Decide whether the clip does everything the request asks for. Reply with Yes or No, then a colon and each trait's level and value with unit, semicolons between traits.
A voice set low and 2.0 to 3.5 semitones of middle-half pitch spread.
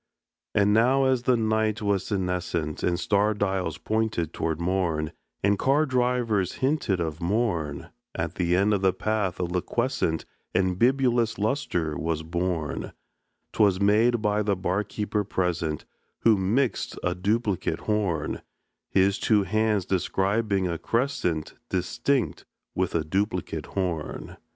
No: very low, 95 Hz; average, 3.9 semitones